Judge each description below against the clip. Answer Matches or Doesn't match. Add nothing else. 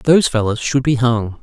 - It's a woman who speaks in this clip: Doesn't match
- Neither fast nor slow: Doesn't match